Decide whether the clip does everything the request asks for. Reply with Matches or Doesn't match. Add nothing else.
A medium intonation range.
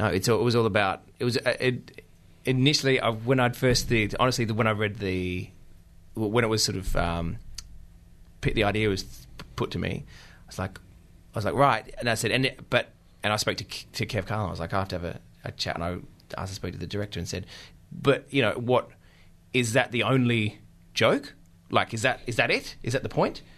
Matches